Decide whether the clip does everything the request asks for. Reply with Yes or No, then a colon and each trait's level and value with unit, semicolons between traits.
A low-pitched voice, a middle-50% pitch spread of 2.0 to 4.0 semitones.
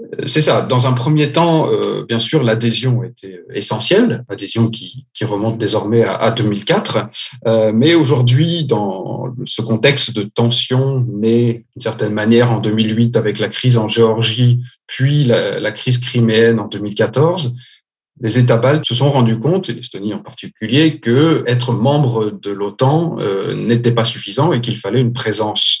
Yes: low, 120 Hz; average, 2.8 semitones